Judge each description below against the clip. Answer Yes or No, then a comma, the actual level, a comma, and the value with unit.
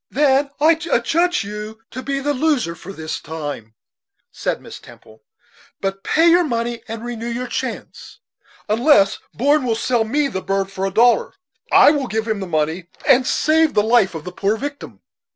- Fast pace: No, average, 180 wpm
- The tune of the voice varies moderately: No, wide, 6.4 semitones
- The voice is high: Yes, high, 230 Hz